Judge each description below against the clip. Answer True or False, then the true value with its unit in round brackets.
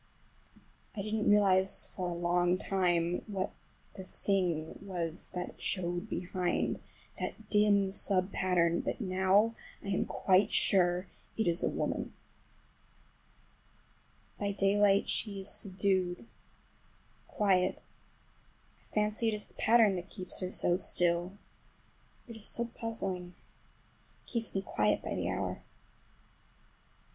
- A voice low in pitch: False (190 Hz)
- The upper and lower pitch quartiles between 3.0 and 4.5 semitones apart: False (2.6 semitones)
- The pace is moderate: False (120 wpm)